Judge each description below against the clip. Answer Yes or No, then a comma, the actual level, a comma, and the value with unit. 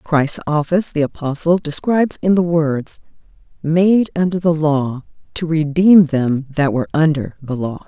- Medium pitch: Yes, medium, 155 Hz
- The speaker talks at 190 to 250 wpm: No, average, 150 wpm